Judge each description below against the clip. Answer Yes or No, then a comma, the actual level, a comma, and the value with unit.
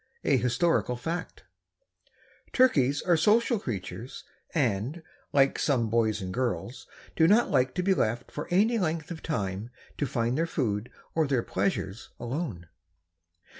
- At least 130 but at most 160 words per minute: Yes, average, 140 wpm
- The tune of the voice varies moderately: No, wide, 6.4 semitones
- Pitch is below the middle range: Yes, low, 130 Hz